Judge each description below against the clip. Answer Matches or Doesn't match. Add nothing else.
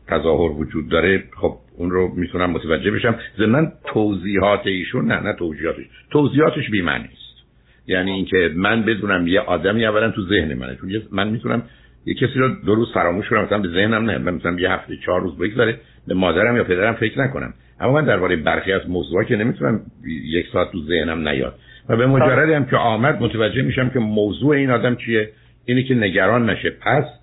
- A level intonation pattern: Doesn't match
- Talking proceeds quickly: Matches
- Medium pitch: Doesn't match